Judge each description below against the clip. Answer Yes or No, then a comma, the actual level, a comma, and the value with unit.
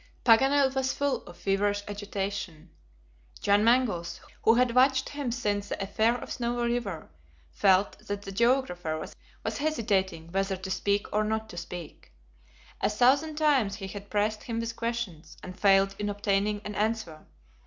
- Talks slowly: No, average, 155 wpm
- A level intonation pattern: No, average, 3.6 semitones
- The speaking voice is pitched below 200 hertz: No, high, 205 Hz